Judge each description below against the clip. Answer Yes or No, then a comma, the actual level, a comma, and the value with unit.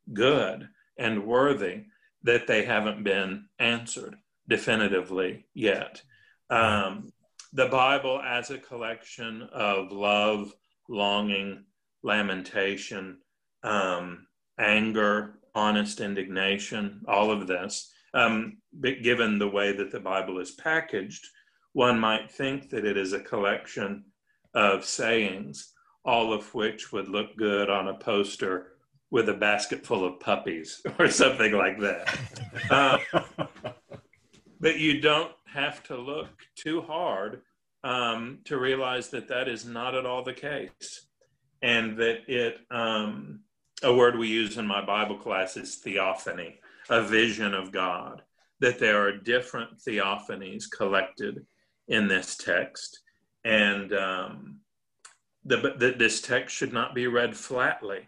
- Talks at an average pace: No, slow, 130 wpm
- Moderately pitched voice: No, low, 110 Hz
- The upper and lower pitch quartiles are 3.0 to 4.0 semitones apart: Yes, average, 3.6 semitones